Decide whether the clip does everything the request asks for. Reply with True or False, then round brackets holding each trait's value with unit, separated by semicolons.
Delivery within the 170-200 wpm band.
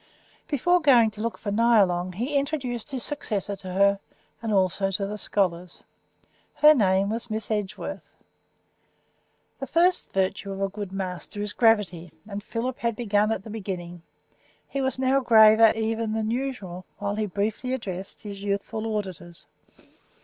False (155 wpm)